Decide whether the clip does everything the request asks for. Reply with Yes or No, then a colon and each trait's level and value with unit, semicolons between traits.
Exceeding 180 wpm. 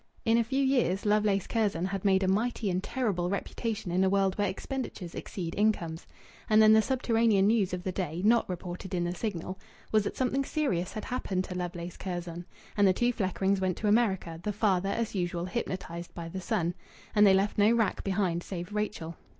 Yes: average, 200 wpm